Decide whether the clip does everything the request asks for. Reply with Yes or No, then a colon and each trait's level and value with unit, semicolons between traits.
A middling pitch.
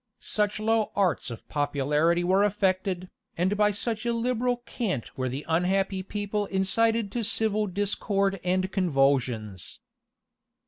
No: high, 195 Hz